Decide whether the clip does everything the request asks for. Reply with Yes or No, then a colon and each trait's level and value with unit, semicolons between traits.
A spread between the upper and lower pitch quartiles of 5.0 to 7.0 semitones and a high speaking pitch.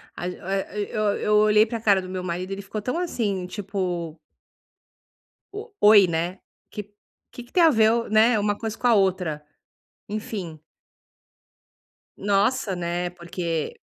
No: average, 3.3 semitones; high, 200 Hz